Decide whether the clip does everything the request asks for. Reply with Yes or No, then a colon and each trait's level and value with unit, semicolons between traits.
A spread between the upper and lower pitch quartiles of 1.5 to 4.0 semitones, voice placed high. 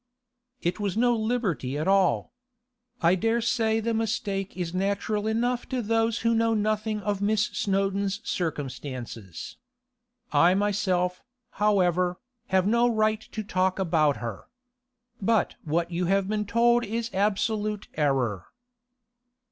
Yes: average, 3.6 semitones; high, 200 Hz